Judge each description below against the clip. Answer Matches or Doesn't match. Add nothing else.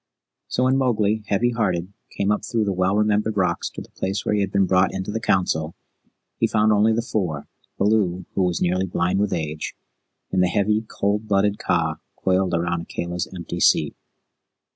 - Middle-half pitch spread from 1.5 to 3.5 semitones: Matches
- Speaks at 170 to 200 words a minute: Matches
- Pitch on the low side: Matches